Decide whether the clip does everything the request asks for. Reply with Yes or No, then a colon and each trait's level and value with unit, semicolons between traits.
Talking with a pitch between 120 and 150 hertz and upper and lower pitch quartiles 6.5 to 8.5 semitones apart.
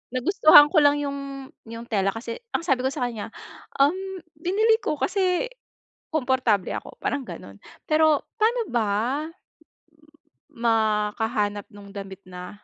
No: very high, 255 Hz; wide, 6.8 semitones